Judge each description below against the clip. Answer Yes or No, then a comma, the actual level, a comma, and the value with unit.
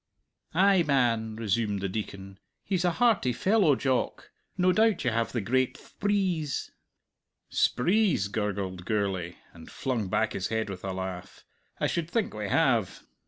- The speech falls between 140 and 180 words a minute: Yes, average, 150 wpm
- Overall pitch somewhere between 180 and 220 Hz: No, low, 115 Hz